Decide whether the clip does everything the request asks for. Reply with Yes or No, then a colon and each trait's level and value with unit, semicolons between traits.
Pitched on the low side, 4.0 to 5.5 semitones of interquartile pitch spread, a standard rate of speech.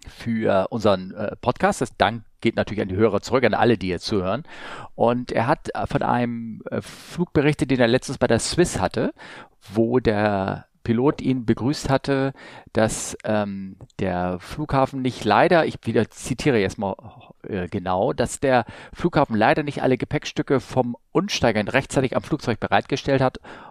Yes: low, 120 Hz; average, 4.5 semitones; average, 155 wpm